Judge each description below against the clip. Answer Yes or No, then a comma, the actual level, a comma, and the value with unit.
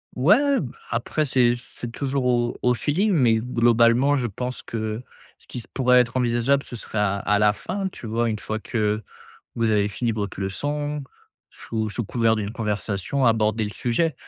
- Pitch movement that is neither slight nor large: Yes, average, 3.1 semitones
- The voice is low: Yes, low, 120 Hz